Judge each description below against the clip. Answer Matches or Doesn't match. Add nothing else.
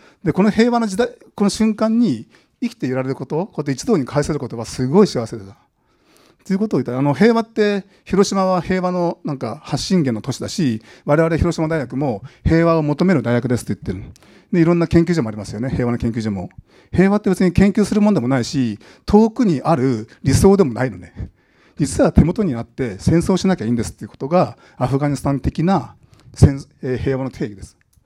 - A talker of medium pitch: Matches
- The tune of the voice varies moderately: Doesn't match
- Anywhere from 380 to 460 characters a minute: Matches